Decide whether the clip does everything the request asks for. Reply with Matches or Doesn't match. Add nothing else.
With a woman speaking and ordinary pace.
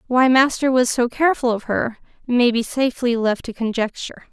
Matches